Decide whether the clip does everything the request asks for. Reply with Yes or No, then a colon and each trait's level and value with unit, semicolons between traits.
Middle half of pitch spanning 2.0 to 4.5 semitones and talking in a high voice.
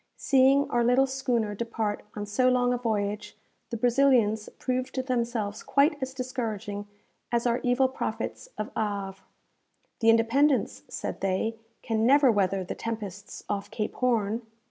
Yes: average, 3.5 semitones; high, 230 Hz